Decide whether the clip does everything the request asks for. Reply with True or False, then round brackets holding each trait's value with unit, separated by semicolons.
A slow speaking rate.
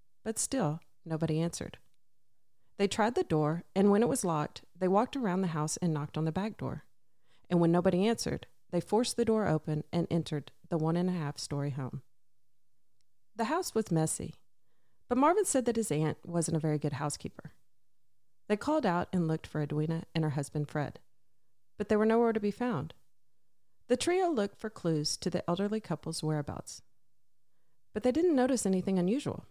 False (185 wpm)